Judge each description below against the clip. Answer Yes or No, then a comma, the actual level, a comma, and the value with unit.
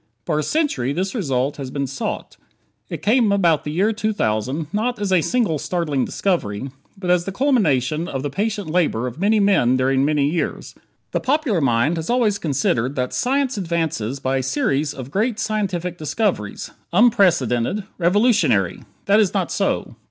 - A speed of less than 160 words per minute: No, average, 165 wpm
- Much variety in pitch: Yes, wide, 7.4 semitones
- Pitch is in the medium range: Yes, medium, 170 Hz